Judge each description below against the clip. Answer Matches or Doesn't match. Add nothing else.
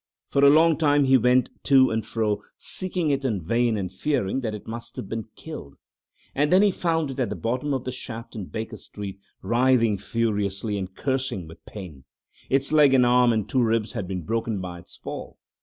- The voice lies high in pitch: Doesn't match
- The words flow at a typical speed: Doesn't match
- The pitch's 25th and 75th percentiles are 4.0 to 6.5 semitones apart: Matches